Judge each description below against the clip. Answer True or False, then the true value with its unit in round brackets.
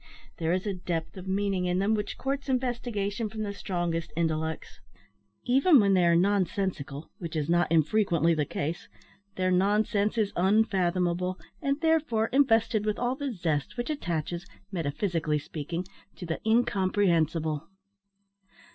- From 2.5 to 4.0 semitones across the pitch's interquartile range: False (4.5 semitones)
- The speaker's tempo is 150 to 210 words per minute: False (140 wpm)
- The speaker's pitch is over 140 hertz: True (190 Hz)